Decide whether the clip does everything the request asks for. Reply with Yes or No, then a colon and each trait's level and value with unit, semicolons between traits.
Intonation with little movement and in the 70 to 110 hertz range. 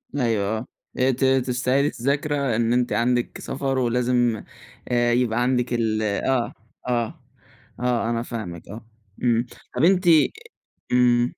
No: narrow, 1.7 semitones; low, 120 Hz